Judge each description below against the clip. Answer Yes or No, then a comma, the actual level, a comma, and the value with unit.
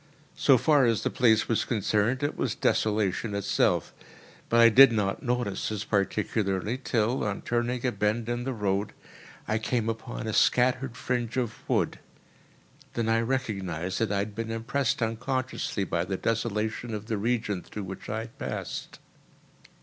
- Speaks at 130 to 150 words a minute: No, average, 165 wpm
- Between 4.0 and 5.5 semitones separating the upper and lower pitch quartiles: No, average, 2.7 semitones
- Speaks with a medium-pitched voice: No, low, 115 Hz